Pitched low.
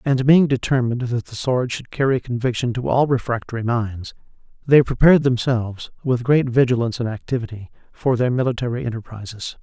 Yes: low, 120 Hz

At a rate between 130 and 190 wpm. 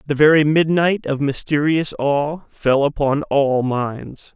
Yes: average, 140 wpm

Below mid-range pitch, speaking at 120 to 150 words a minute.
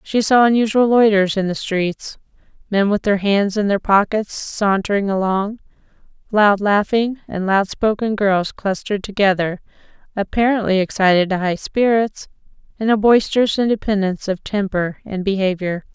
No: high, 205 Hz; average, 140 wpm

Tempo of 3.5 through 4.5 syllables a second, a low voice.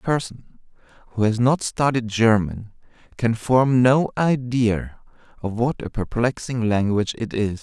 Yes: 4.3 syllables/s; low, 115 Hz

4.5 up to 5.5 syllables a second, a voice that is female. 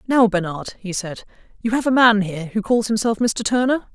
Yes: 5.4 syllables/s; female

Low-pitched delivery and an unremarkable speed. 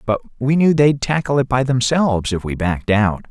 No: low, 125 Hz; fast, 220 wpm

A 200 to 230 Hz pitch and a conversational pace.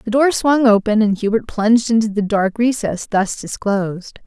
Yes: high, 220 Hz; average, 185 wpm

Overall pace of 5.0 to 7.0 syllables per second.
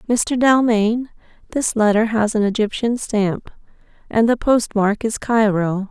No: 4.0 syllables/s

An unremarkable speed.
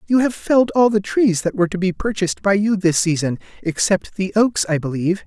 No: fast, 230 wpm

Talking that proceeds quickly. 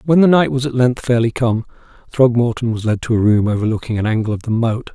Yes: fast, 245 wpm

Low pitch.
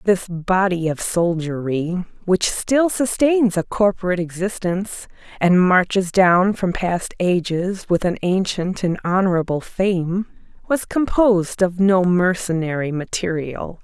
No: medium, 185 Hz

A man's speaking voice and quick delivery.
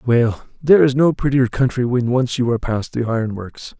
Yes: male; fast, 220 wpm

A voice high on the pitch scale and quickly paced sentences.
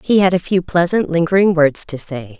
No: medium, 170 Hz; fast, 225 wpm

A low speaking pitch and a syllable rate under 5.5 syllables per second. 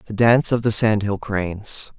Yes: low, 110 Hz; 5.1 syllables/s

